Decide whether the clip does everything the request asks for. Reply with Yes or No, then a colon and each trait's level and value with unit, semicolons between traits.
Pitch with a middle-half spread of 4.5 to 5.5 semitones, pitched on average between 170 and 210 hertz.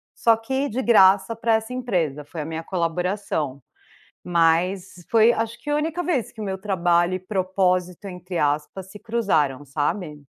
Yes: average, 5.0 semitones; high, 190 Hz